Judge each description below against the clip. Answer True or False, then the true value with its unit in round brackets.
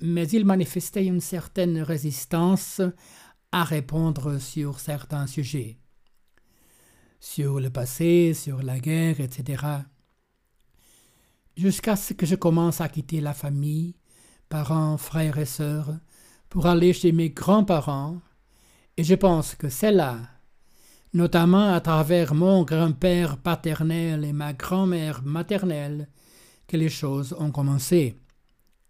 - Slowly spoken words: True (120 wpm)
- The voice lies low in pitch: False (160 Hz)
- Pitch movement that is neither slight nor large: True (3.3 semitones)